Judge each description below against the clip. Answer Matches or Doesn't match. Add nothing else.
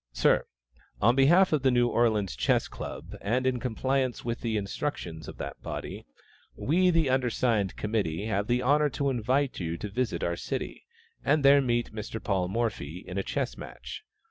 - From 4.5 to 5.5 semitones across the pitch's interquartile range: Matches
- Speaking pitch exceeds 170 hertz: Doesn't match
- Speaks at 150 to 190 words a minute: Matches